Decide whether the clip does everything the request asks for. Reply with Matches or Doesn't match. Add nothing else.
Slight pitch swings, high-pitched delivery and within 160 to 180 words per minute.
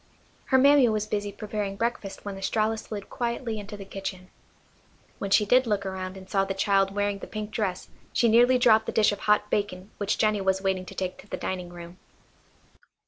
Doesn't match